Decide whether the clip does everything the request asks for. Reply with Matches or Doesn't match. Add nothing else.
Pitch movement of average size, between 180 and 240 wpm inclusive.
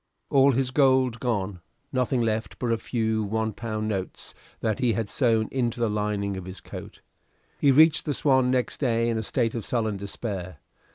Matches